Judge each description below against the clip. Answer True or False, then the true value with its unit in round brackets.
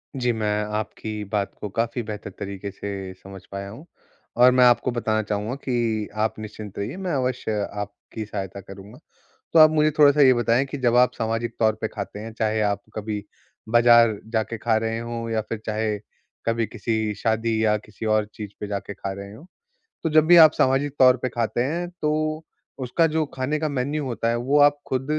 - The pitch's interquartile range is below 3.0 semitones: False (3.3 semitones)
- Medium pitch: False (115 Hz)